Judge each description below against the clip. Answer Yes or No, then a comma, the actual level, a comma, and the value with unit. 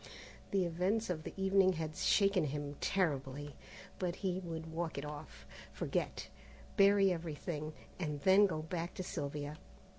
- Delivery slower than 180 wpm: Yes, average, 145 wpm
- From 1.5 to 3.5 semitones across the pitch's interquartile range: No, average, 3.9 semitones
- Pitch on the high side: No, medium, 165 Hz